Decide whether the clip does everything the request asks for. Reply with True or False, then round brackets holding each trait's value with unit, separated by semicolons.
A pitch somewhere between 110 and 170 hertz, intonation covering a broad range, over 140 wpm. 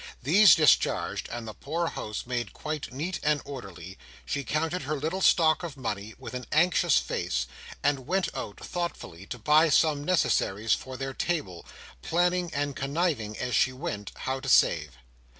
True (140 Hz; 5.9 semitones; 165 wpm)